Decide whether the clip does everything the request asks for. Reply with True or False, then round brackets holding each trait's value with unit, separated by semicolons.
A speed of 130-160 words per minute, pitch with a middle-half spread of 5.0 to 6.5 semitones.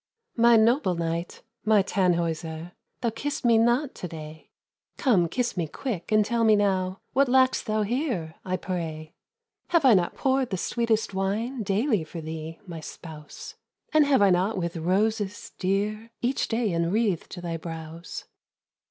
True (155 wpm; 5.5 semitones)